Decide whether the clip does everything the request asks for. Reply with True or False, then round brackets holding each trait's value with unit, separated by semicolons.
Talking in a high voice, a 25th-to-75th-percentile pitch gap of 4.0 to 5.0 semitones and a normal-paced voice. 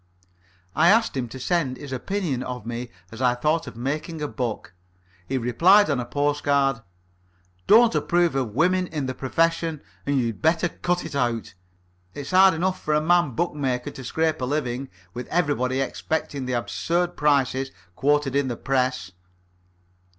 False (140 Hz; 4.5 semitones; 165 wpm)